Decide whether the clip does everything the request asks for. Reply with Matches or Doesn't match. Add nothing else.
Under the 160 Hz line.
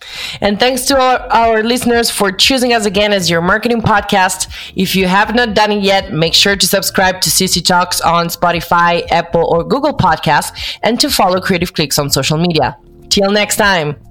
Doesn't match